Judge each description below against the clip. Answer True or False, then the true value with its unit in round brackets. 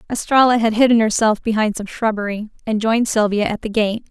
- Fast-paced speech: False (190 wpm)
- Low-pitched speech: False (220 Hz)